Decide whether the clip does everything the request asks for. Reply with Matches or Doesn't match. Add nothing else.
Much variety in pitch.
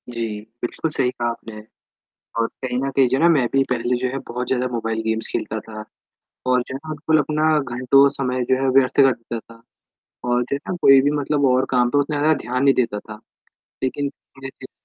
Doesn't match